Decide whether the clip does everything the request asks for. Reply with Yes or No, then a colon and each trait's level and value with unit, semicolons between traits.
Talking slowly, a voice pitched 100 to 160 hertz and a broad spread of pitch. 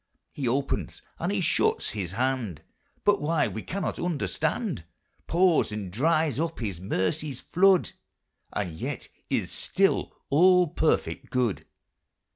Yes: slow, 125 wpm; medium, 140 Hz; wide, 7.8 semitones